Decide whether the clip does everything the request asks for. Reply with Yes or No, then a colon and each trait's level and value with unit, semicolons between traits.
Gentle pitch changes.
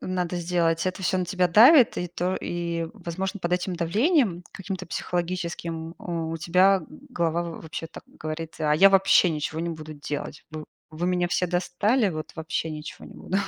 Yes: narrow, 2.2 semitones